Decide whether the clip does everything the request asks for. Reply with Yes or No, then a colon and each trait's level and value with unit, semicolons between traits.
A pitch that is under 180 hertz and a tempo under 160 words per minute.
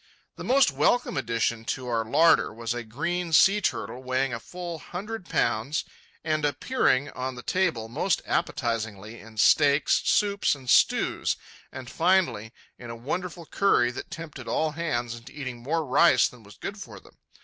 No: low, 135 Hz; average, 165 wpm